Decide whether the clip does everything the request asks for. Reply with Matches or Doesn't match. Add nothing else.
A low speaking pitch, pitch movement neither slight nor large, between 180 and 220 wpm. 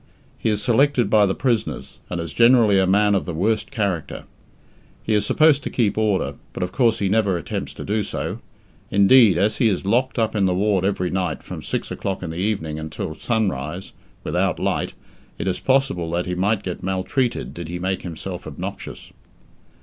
Matches